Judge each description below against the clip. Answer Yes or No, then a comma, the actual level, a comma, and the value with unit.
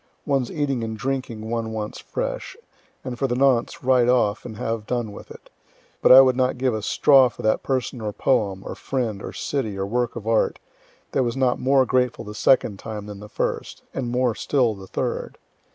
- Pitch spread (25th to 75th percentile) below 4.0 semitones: Yes, average, 3.2 semitones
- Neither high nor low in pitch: No, low, 120 Hz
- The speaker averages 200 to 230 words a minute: Yes, fast, 205 wpm